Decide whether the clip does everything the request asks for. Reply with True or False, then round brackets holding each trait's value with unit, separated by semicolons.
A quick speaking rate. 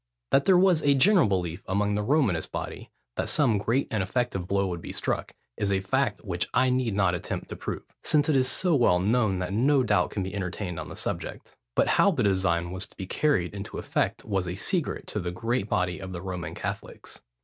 True (225 wpm)